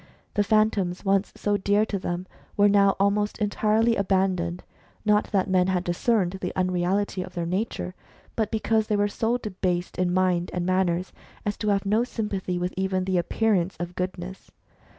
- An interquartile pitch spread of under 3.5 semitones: Yes, narrow, 2.4 semitones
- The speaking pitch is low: No, high, 190 Hz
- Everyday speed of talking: Yes, average, 175 wpm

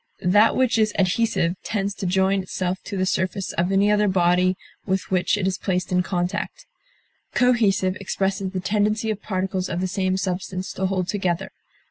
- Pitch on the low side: No, high, 190 Hz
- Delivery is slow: No, average, 175 wpm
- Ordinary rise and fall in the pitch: No, narrow, 1.7 semitones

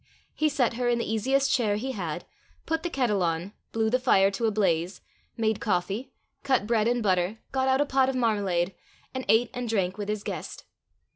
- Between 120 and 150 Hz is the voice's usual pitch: No, high, 225 Hz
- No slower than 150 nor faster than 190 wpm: No, fast, 205 wpm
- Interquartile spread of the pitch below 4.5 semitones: No, average, 4.8 semitones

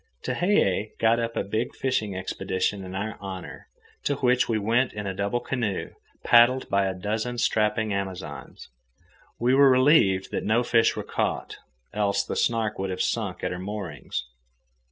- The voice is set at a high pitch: No, low, 105 Hz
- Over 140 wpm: Yes, average, 165 wpm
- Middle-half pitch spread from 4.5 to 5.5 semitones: No, average, 3.7 semitones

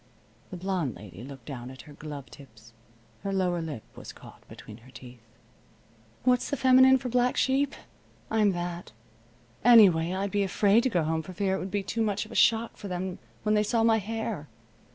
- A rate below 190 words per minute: No, average, 195 wpm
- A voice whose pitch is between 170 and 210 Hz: Yes, high, 190 Hz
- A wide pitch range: Yes, wide, 6.5 semitones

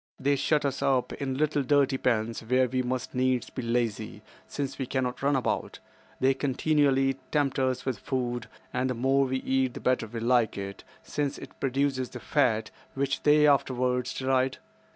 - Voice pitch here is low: Yes, low, 130 Hz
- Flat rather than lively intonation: Yes, narrow, 1.8 semitones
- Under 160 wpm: No, average, 175 wpm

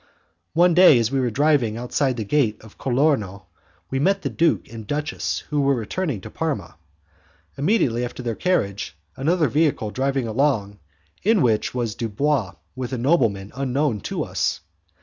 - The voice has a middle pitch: No, low, 130 Hz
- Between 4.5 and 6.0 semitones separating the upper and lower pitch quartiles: Yes, average, 5.2 semitones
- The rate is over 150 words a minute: Yes, average, 160 wpm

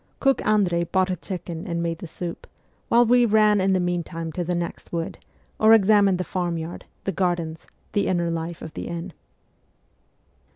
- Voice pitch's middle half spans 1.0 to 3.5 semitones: Yes, average, 2.8 semitones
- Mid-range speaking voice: Yes, medium, 175 Hz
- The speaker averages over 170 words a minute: Yes, average, 180 wpm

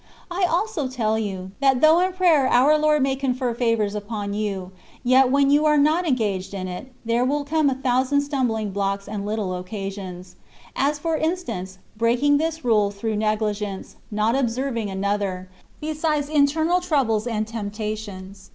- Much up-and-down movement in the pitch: Yes, wide, 6.0 semitones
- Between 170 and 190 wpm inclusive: No, average, 160 wpm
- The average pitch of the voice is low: No, high, 235 Hz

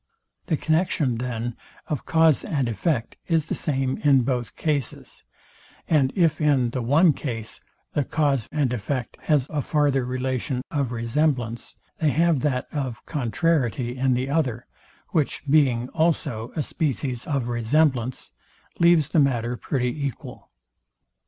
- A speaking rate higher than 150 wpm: No, average, 140 wpm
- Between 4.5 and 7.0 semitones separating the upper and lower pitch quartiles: No, average, 3.7 semitones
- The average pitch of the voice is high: No, low, 135 Hz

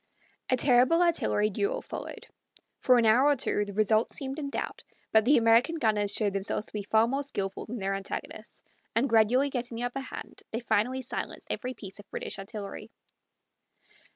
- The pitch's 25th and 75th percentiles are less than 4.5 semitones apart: Yes, average, 4.1 semitones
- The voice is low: No, high, 230 Hz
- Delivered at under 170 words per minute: No, average, 180 wpm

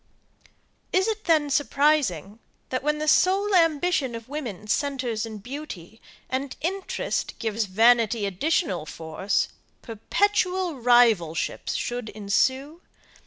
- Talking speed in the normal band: No, slow, 110 wpm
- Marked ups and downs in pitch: Yes, wide, 6.4 semitones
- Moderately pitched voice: No, very high, 255 Hz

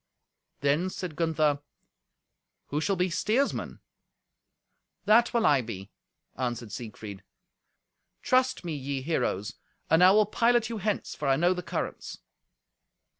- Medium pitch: Yes, medium, 165 Hz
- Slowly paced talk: Yes, slow, 125 wpm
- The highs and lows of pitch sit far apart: Yes, wide, 7.7 semitones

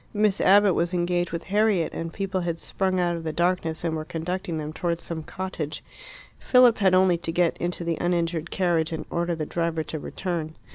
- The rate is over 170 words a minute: Yes, average, 200 wpm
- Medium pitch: Yes, medium, 175 Hz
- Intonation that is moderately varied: No, narrow, 2.1 semitones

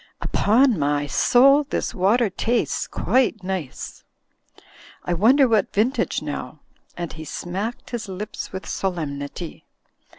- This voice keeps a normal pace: No, slow, 120 wpm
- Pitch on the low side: No, high, 195 Hz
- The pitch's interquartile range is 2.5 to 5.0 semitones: No, wide, 5.6 semitones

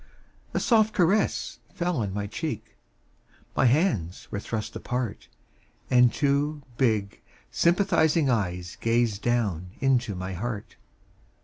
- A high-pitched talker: No, low, 120 Hz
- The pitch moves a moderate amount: No, wide, 6.8 semitones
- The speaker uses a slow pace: Yes, slow, 115 wpm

